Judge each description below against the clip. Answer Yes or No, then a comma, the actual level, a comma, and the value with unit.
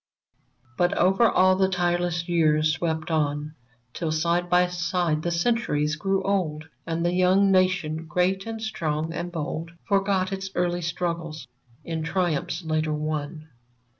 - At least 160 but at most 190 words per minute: No, average, 140 wpm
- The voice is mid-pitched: Yes, medium, 175 Hz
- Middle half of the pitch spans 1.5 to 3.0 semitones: Yes, average, 2.7 semitones